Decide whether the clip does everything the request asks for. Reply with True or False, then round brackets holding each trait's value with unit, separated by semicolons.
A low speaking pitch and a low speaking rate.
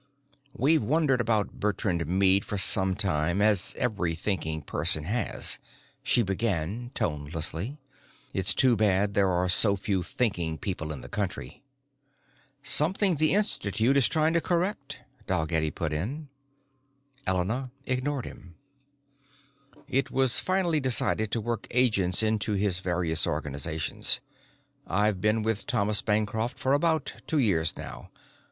True (105 Hz; 130 wpm)